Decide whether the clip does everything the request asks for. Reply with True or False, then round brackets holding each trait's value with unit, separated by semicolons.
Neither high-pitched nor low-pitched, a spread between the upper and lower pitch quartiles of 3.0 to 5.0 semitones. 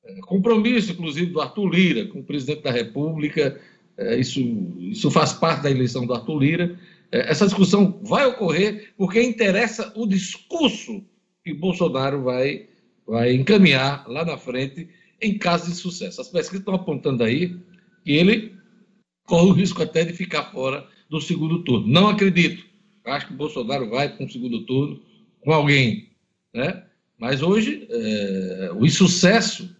False (175 Hz; 5.5 semitones)